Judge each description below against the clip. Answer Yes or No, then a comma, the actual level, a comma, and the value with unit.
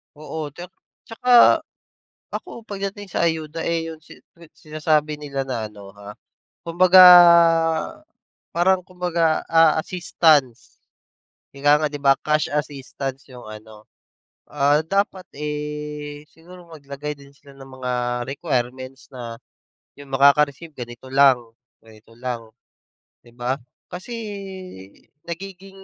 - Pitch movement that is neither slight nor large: Yes, average, 4.0 semitones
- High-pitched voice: No, medium, 150 Hz